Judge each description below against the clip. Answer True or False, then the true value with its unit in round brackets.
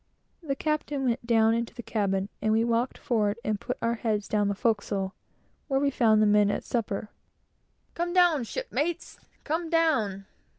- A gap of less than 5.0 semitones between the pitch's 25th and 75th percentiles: False (5.3 semitones)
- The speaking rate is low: False (170 wpm)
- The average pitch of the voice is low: False (230 Hz)